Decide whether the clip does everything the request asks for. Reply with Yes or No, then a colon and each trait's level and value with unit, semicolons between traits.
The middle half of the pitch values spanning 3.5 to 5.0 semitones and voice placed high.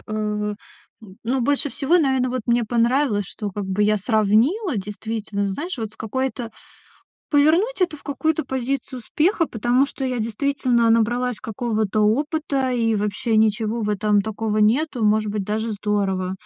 Yes: average, 4.1 semitones; high, 230 Hz